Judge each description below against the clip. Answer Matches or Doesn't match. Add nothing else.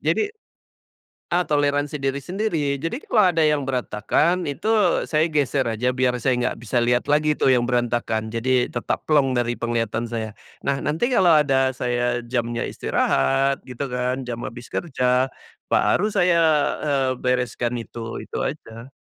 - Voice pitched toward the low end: Matches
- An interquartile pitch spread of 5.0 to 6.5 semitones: Doesn't match